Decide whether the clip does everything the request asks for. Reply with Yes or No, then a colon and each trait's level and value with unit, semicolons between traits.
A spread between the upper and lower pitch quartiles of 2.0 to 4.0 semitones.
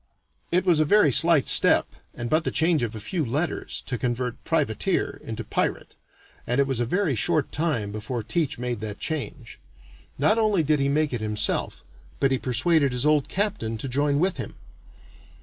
No: average, 4.9 semitones